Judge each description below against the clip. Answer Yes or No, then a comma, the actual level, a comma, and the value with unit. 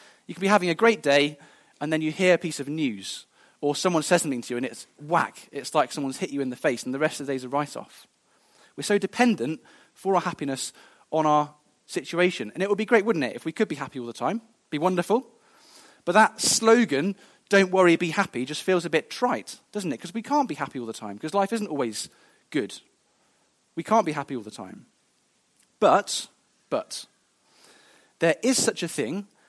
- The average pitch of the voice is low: No, medium, 170 Hz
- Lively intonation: Yes, wide, 6.9 semitones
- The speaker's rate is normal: No, fast, 220 wpm